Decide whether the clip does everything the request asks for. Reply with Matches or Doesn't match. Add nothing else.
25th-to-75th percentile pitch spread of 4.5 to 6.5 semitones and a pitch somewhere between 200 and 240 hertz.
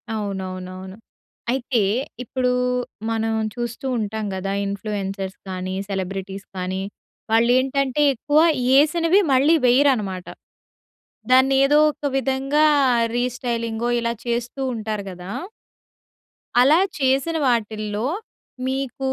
Matches